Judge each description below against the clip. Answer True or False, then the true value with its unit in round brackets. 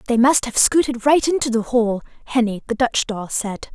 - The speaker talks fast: True (210 wpm)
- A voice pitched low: False (240 Hz)